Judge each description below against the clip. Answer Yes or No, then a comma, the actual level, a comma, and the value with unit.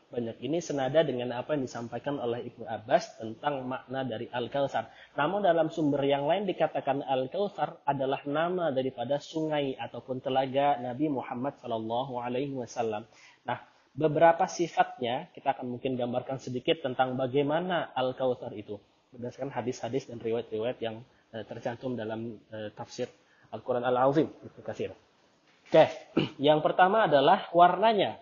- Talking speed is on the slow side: No, average, 125 wpm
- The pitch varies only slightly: No, average, 3.5 semitones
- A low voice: Yes, low, 130 Hz